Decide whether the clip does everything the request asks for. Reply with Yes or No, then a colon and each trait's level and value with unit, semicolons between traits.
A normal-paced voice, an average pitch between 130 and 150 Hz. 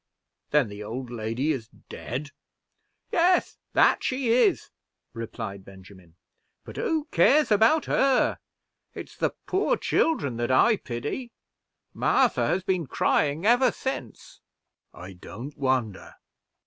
No: slow, 120 wpm; medium, 140 Hz